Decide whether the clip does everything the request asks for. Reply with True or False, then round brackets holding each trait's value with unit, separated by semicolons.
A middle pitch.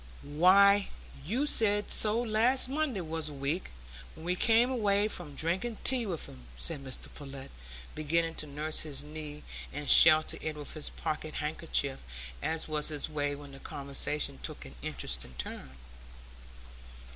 True (155 Hz)